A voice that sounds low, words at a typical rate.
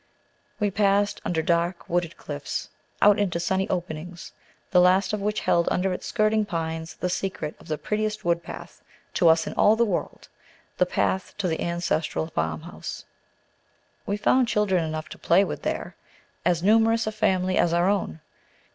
No: medium, 180 Hz; average, 165 wpm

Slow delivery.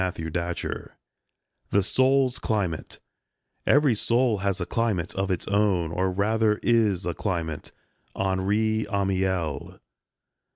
Yes: slow, 130 wpm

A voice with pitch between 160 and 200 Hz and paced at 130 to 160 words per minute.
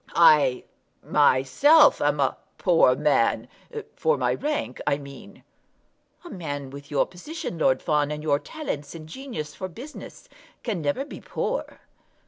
No: medium, 150 Hz; average, 140 wpm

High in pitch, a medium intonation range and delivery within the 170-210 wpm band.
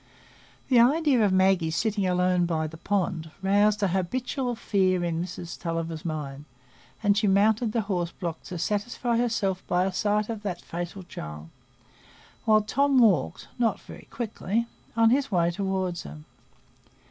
No: high, 195 Hz; average, 4.1 semitones; average, 145 wpm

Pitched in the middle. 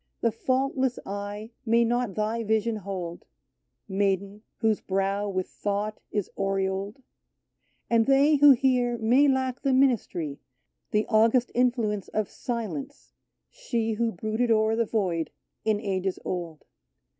No: high, 220 Hz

